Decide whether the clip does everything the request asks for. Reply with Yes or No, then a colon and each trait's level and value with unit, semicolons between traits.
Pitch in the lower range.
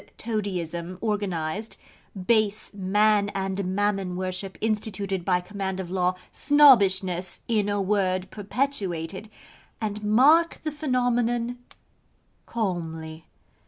No: high, 200 Hz